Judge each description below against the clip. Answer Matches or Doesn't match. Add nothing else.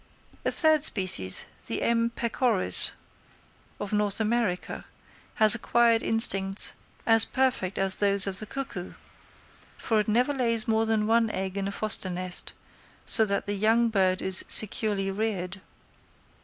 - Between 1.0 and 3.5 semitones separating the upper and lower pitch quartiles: Matches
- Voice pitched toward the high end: Matches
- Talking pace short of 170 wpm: Matches